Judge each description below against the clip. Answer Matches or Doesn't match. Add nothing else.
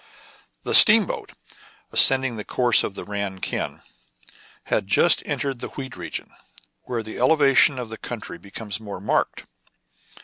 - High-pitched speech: Doesn't match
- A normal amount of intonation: Matches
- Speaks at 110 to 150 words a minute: Matches